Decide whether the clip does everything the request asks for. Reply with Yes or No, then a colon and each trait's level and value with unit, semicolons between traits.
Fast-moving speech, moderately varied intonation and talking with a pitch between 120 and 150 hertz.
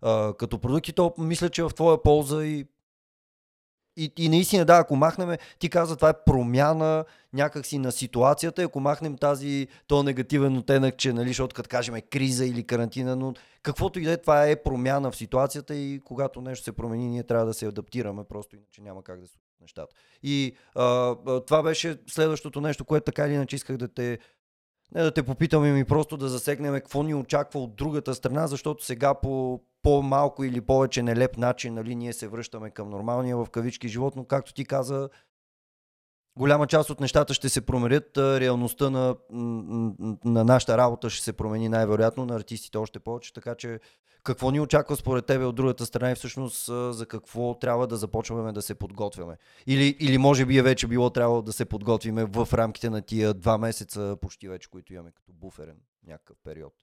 Yes: fast, 190 wpm; average, 3.7 semitones; low, 130 Hz